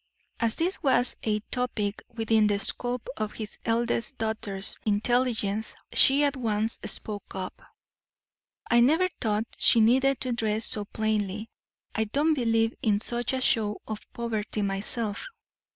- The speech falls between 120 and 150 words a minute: Yes, average, 140 wpm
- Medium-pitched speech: No, high, 225 Hz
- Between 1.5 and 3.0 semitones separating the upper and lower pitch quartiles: Yes, narrow, 2.5 semitones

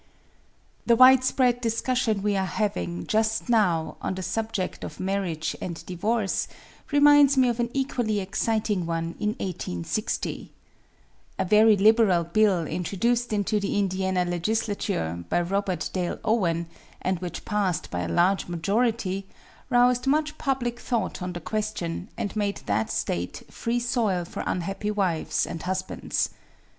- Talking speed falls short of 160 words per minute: Yes, average, 140 wpm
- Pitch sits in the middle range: No, high, 200 Hz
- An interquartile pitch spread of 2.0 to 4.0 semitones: No, average, 4.5 semitones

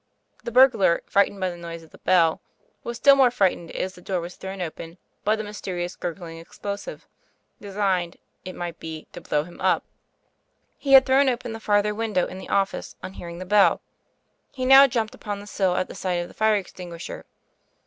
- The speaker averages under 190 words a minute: No, average, 200 wpm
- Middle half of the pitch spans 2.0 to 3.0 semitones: No, average, 3.8 semitones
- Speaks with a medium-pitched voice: No, high, 195 Hz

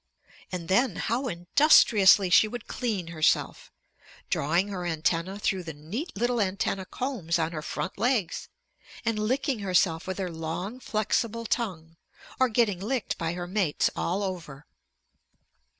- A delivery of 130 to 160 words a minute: Yes, average, 140 wpm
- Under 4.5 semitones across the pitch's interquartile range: No, average, 5.3 semitones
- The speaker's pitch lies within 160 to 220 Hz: Yes, high, 190 Hz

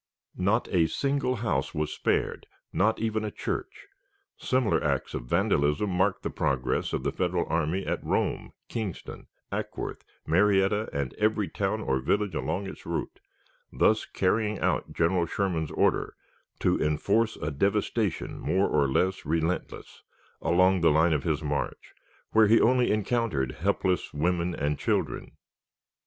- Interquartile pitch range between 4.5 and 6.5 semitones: Yes, average, 5.2 semitones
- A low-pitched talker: Yes, very low, 95 Hz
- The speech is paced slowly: No, average, 145 wpm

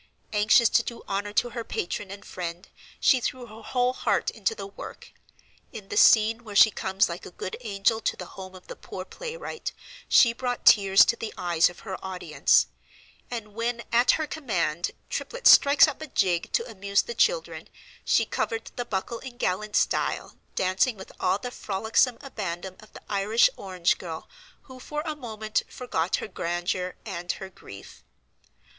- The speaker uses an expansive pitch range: No, average, 4.6 semitones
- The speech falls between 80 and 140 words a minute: No, average, 180 wpm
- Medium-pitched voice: No, high, 215 Hz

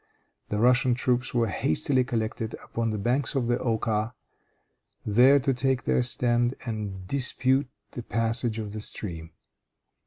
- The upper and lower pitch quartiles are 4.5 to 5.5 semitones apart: No, average, 2.7 semitones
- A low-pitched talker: Yes, low, 120 Hz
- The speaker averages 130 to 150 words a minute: Yes, average, 145 wpm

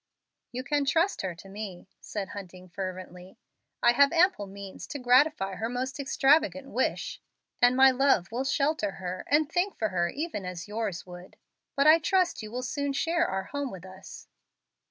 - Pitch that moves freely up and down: Yes, wide, 6.9 semitones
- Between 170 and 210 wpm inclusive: Yes, average, 175 wpm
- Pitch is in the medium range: No, high, 245 Hz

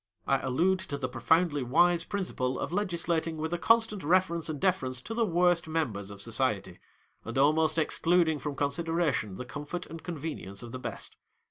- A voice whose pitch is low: No, medium, 160 Hz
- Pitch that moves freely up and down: No, average, 5.0 semitones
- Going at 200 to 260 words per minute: No, average, 175 wpm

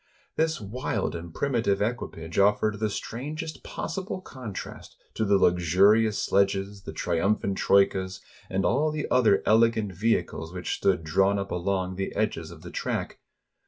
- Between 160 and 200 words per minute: No, average, 150 wpm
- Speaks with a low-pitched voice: Yes, low, 100 Hz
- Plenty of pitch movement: No, average, 3.4 semitones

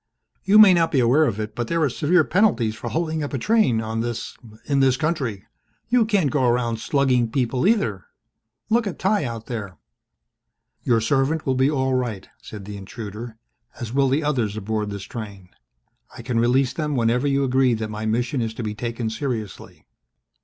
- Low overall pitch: Yes, low, 125 Hz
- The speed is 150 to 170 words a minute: No, average, 190 wpm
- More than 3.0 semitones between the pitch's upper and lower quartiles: Yes, average, 4.6 semitones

